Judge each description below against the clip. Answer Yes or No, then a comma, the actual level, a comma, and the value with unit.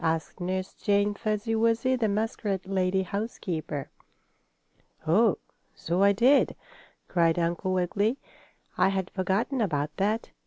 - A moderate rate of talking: No, slow, 120 wpm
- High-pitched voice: Yes, high, 195 Hz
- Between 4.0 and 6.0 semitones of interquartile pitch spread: No, average, 3.6 semitones